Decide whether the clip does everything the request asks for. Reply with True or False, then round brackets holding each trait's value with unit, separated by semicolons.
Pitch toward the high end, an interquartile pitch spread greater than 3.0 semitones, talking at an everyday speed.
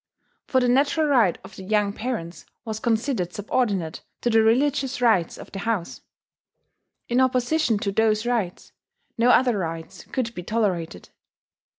True (225 Hz; 4.6 semitones; 150 wpm)